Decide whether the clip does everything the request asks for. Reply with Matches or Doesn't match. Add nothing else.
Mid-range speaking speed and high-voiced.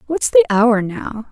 Matches